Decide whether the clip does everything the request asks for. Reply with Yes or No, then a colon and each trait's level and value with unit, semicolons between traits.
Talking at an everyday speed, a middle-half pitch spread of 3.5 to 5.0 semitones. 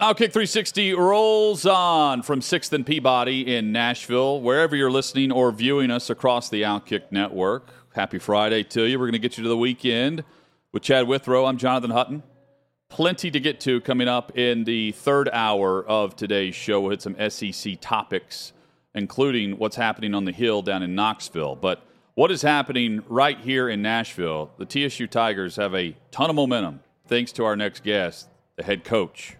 Yes: average, 180 wpm; average, 4.6 semitones